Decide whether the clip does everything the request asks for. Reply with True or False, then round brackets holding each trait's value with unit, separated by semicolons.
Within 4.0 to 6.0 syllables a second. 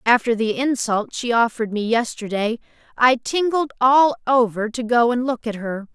True (4.8 syllables/s)